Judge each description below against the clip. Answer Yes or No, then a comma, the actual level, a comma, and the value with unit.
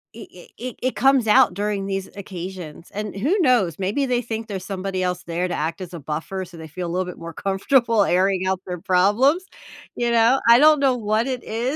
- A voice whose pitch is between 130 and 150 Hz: No, high, 195 Hz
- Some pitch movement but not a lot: Yes, average, 4.7 semitones